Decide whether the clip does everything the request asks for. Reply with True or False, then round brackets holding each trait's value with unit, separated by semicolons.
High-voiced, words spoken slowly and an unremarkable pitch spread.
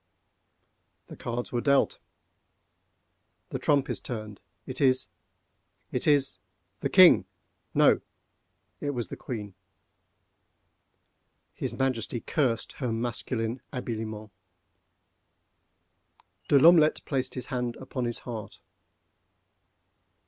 False (125 Hz; 85 wpm; 3.2 semitones)